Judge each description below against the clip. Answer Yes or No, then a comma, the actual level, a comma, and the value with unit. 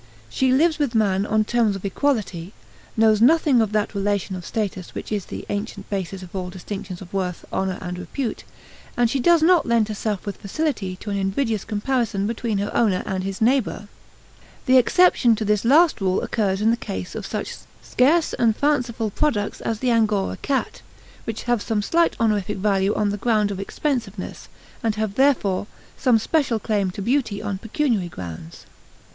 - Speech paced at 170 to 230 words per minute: Yes, average, 180 wpm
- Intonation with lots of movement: No, average, 3.6 semitones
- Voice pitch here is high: Yes, high, 215 Hz